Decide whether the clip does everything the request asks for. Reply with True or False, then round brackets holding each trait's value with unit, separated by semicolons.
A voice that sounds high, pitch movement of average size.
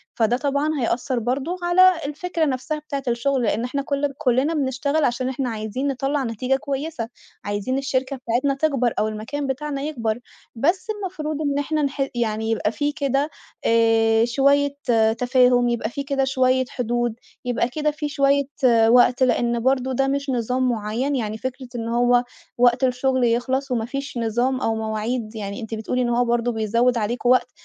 True (255 Hz; 3.1 semitones)